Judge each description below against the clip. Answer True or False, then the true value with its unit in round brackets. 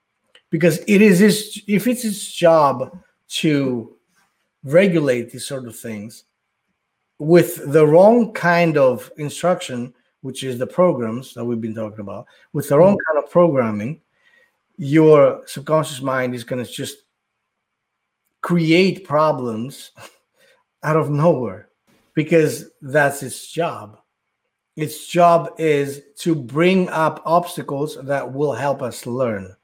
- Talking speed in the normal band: False (130 wpm)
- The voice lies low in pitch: False (155 Hz)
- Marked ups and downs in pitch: False (5.0 semitones)